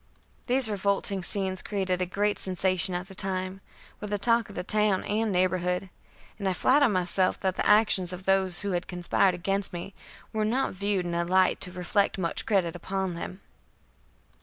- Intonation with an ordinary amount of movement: No, narrow, 1.9 semitones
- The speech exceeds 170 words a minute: Yes, average, 185 wpm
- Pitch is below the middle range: No, high, 190 Hz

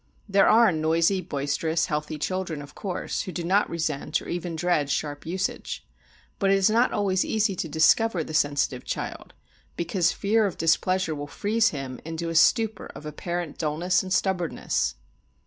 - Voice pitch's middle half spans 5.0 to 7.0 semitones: No, average, 3.8 semitones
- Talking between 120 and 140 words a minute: No, average, 165 wpm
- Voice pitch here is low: No, medium, 170 Hz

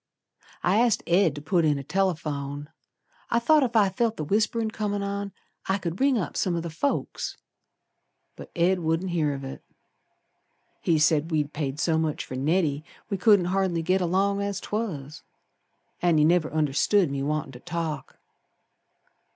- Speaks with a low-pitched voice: No, medium, 170 Hz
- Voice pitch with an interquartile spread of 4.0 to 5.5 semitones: Yes, average, 4.7 semitones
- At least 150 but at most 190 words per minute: Yes, average, 165 wpm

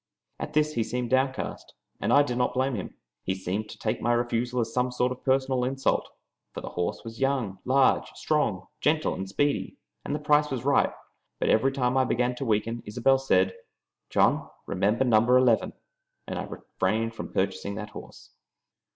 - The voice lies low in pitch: Yes, low, 125 Hz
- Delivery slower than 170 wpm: No, average, 185 wpm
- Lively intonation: No, average, 3.5 semitones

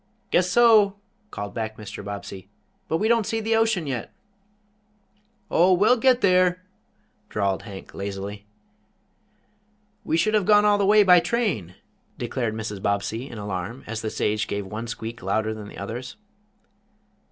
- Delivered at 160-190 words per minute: No, average, 150 wpm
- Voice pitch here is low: Yes, low, 115 Hz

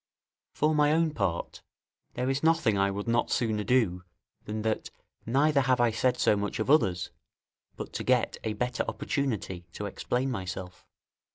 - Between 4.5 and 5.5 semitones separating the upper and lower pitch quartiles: Yes, average, 4.9 semitones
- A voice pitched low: Yes, low, 115 Hz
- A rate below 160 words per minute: No, average, 165 wpm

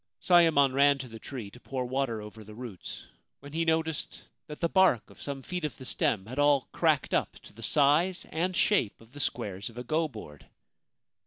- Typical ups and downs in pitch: No, wide, 5.7 semitones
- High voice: No, low, 135 Hz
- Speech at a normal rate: No, fast, 210 wpm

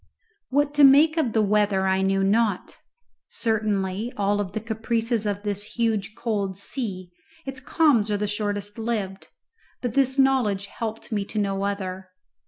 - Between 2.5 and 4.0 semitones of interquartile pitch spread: Yes, average, 2.9 semitones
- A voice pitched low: No, high, 210 Hz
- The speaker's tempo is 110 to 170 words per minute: Yes, average, 160 wpm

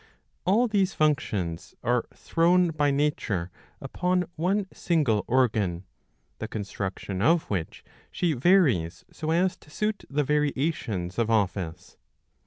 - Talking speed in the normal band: No, slow, 120 wpm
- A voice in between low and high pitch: Yes, medium, 145 Hz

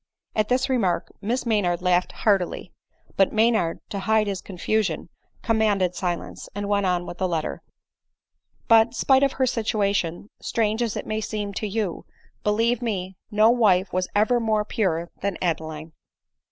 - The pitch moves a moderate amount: Yes, average, 3.4 semitones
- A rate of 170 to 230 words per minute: No, average, 160 wpm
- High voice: Yes, high, 205 Hz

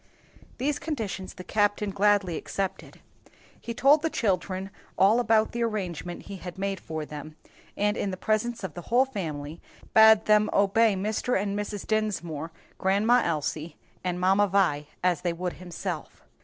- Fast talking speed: No, average, 155 wpm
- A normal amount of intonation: Yes, average, 3.5 semitones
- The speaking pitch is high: Yes, high, 195 Hz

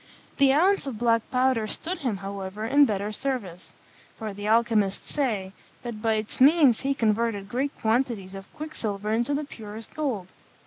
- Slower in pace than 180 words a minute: Yes, average, 165 wpm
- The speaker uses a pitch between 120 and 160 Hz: No, high, 230 Hz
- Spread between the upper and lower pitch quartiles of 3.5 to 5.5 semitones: Yes, average, 4.6 semitones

